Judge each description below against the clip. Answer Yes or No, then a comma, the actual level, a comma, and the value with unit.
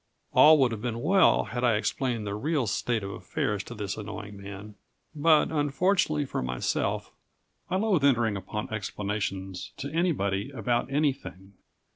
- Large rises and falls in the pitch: Yes, wide, 6.3 semitones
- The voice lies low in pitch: Yes, low, 115 Hz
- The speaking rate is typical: Yes, average, 150 wpm